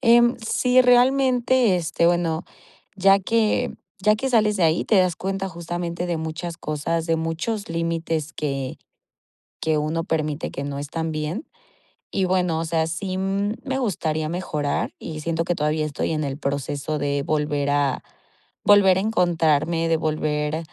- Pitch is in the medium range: Yes, medium, 165 Hz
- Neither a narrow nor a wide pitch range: Yes, average, 4.1 semitones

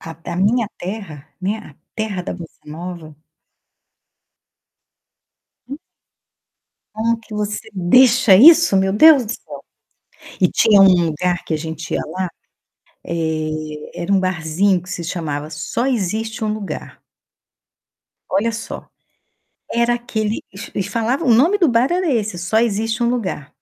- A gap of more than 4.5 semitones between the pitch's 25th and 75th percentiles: Yes, average, 5.0 semitones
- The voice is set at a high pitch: Yes, high, 200 Hz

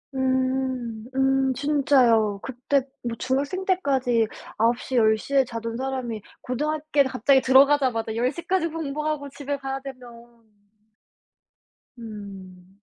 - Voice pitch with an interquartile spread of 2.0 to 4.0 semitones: Yes, average, 3.4 semitones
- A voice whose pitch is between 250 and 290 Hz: Yes, very high, 260 Hz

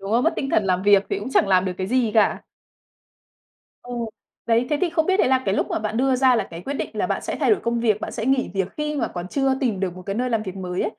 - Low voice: No, high, 230 Hz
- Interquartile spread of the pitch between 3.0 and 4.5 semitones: No, average, 5.2 semitones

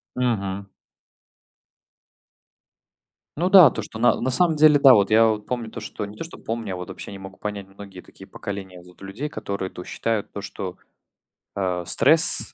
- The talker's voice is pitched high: No, low, 105 Hz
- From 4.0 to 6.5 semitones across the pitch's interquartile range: Yes, average, 4.3 semitones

